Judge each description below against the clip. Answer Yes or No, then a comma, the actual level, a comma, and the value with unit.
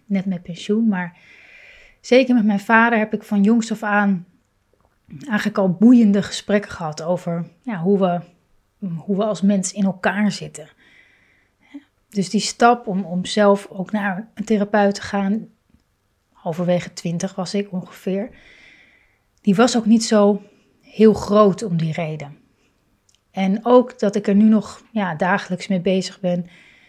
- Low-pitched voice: No, high, 200 Hz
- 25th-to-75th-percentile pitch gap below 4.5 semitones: Yes, average, 2.8 semitones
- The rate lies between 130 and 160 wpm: Yes, average, 155 wpm